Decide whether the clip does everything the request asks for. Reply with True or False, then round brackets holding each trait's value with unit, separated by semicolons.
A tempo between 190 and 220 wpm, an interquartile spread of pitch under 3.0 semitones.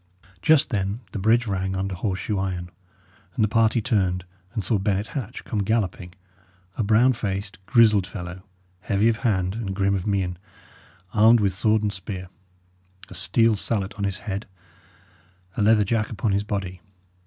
False (165 wpm; 2.6 semitones)